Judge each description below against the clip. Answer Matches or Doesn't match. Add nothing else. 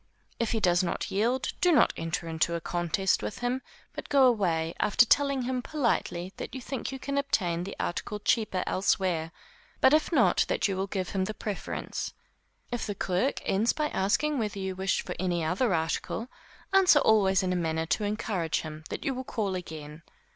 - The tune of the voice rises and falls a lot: Matches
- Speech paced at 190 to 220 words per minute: Matches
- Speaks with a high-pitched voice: Matches